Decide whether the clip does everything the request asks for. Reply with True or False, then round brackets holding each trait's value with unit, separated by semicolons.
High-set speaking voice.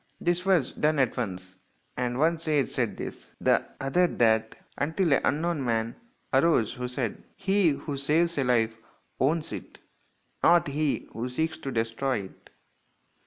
False (140 Hz)